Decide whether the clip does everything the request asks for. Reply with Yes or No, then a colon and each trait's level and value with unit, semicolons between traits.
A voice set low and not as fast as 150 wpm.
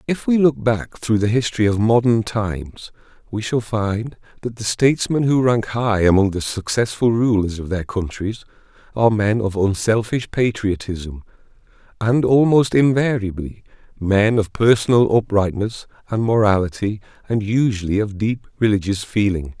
Yes: low, 110 Hz; average, 140 wpm